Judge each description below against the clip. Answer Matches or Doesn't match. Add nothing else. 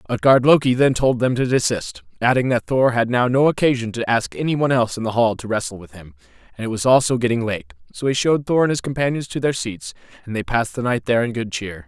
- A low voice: Matches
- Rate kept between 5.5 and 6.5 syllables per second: Matches